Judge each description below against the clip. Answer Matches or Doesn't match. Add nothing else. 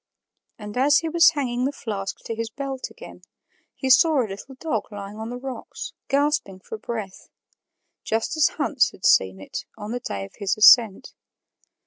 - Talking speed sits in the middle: Matches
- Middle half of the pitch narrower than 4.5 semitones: Doesn't match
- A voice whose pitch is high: Matches